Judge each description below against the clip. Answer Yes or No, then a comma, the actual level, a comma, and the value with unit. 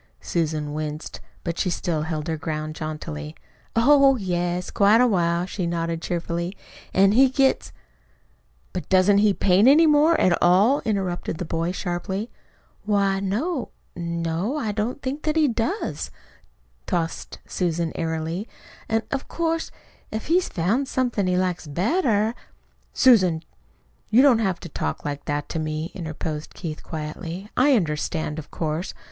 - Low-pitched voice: No, medium, 180 Hz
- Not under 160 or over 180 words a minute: No, average, 150 wpm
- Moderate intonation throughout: No, wide, 5.7 semitones